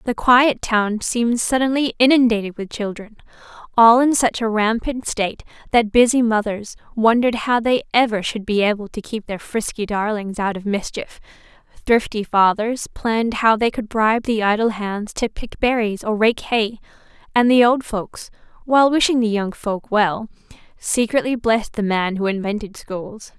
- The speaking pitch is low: No, high, 220 Hz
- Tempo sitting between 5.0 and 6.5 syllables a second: No, 4.8 syllables/s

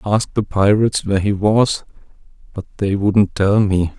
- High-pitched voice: No, low, 100 Hz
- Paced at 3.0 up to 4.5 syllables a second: No, 5.3 syllables/s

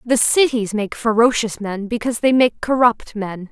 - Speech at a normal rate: Yes, average, 170 wpm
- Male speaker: No, female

